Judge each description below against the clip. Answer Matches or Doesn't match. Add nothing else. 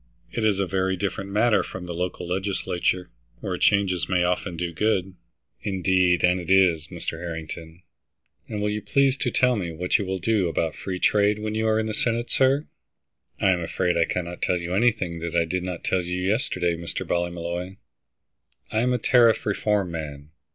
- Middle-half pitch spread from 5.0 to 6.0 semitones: Doesn't match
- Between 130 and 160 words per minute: Doesn't match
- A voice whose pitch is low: Matches